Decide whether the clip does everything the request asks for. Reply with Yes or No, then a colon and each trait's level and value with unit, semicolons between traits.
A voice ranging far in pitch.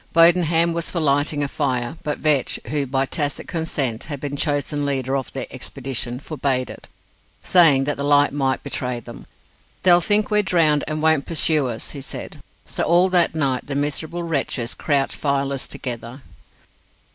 No: average, 3.0 semitones